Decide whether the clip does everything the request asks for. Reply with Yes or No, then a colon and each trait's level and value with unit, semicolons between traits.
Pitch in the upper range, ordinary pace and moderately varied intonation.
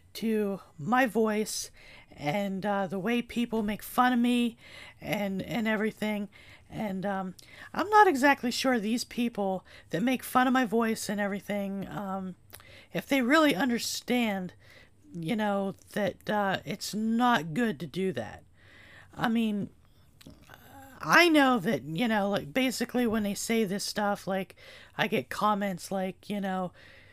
Yes: high, 205 Hz; average, 150 wpm; average, 3.8 semitones